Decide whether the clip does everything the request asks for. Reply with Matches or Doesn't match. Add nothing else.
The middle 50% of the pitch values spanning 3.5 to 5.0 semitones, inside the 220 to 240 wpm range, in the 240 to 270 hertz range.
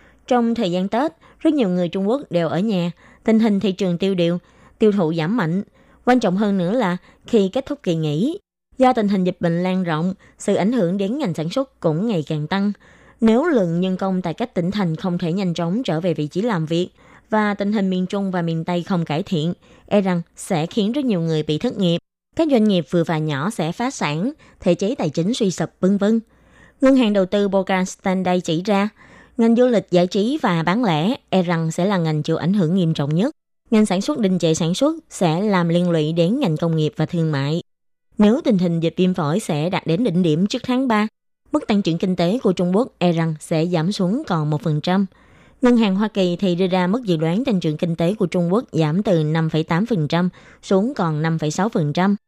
Doesn't match